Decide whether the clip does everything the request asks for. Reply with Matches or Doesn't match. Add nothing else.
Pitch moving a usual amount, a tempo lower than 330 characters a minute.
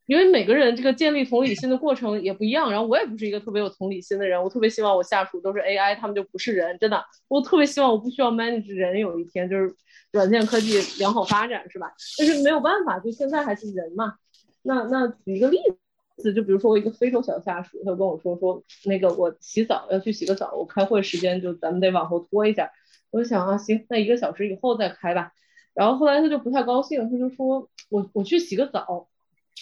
Doesn't match